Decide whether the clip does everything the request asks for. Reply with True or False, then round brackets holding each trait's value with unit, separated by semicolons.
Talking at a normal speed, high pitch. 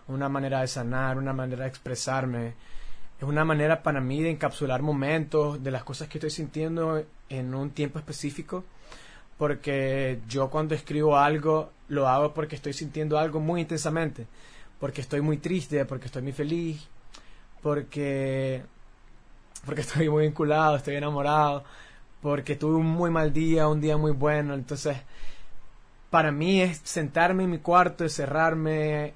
False (150 wpm; 150 Hz)